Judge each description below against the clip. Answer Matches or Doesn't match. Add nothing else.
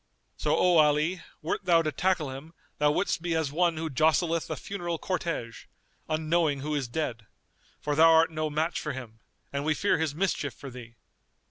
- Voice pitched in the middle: Matches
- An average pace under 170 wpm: Doesn't match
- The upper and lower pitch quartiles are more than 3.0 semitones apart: Doesn't match